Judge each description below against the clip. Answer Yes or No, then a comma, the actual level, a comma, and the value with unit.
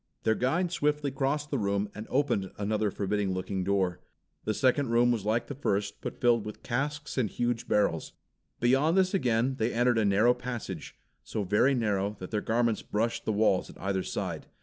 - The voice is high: No, low, 115 Hz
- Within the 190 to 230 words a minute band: Yes, average, 195 wpm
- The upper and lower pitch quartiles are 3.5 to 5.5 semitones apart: Yes, average, 4.3 semitones